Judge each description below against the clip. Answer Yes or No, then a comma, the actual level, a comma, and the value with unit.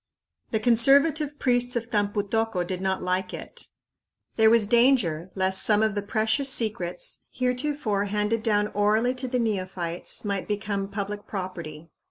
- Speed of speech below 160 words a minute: Yes, average, 150 wpm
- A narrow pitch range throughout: No, average, 3.7 semitones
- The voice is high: Yes, high, 210 Hz